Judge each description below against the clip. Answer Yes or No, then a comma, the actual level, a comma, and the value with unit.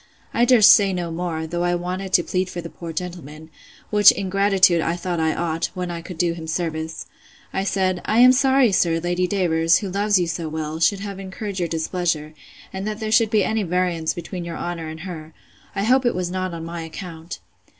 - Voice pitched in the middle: Yes, medium, 175 Hz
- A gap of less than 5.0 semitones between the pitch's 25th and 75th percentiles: Yes, average, 3.0 semitones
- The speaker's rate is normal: No, fast, 220 wpm